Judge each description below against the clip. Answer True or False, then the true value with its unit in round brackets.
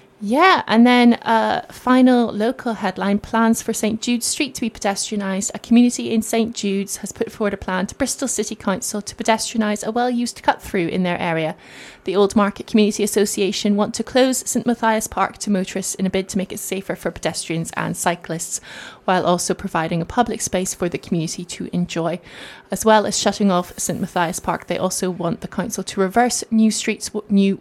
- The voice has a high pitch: True (205 Hz)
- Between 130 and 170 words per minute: False (200 wpm)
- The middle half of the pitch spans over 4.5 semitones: False (3.2 semitones)